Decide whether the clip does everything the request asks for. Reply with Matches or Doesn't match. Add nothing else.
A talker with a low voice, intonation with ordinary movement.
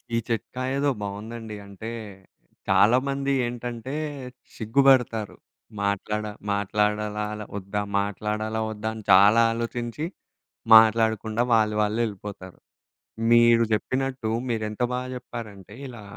Doesn't match